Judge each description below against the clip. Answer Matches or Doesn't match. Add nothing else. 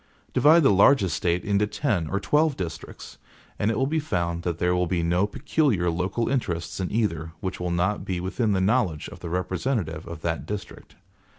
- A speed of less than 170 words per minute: Doesn't match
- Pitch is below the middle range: Matches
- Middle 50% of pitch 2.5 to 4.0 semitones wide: Doesn't match